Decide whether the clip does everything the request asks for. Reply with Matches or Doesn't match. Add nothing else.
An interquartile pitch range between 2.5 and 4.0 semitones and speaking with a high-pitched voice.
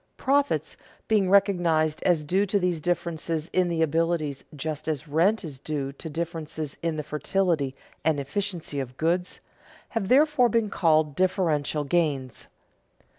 Doesn't match